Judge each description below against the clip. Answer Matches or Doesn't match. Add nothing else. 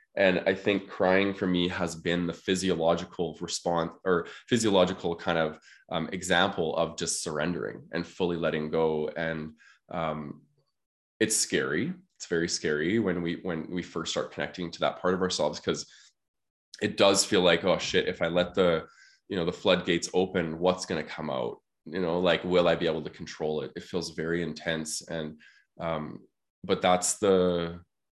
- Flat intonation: Matches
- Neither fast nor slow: Matches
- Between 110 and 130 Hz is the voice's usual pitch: Doesn't match